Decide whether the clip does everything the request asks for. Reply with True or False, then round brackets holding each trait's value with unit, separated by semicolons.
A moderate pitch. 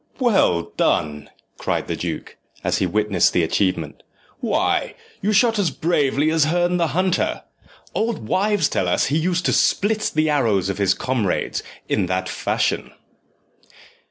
True (150 Hz)